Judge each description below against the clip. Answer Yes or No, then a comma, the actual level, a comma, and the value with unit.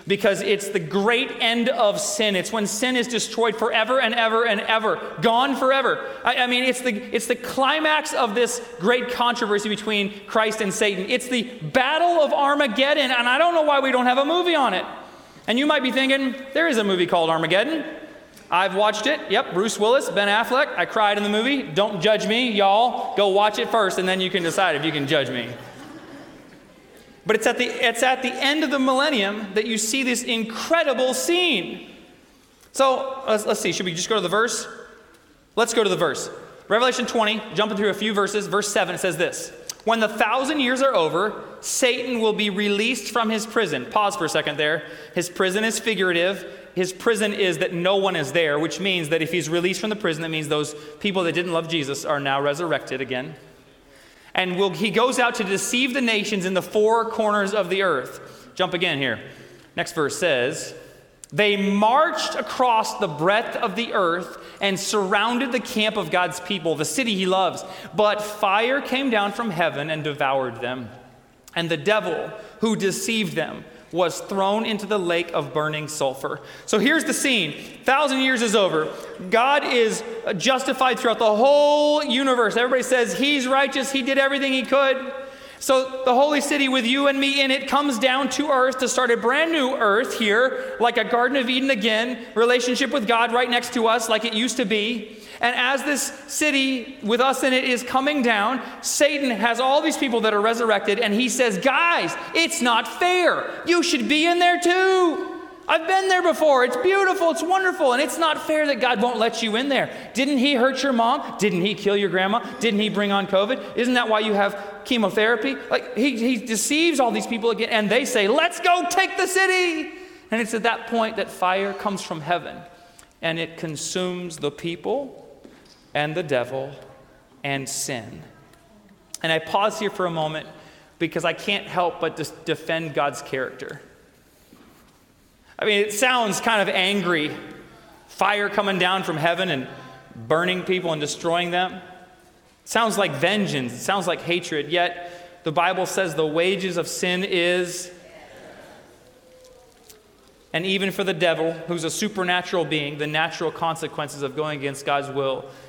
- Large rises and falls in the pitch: Yes, wide, 6.3 semitones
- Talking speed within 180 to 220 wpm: Yes, average, 190 wpm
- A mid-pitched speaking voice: No, high, 220 Hz